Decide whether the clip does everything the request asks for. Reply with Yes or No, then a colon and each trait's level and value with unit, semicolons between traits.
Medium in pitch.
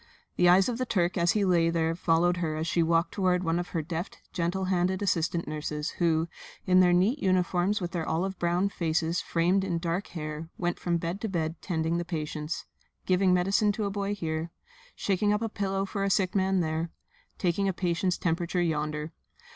Yes: medium, 175 Hz